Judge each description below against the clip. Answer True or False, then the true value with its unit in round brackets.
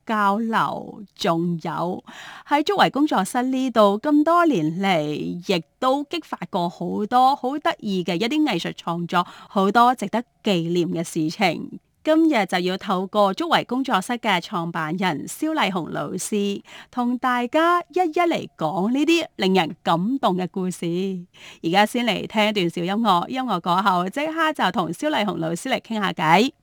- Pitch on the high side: True (205 Hz)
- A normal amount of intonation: False (6.6 semitones)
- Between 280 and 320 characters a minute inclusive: False (235 characters per minute)